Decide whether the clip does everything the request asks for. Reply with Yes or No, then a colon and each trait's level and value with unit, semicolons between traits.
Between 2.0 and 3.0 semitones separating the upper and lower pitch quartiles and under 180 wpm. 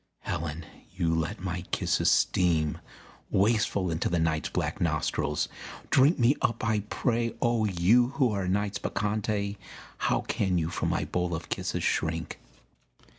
No: average, 4.5 semitones; average, 145 wpm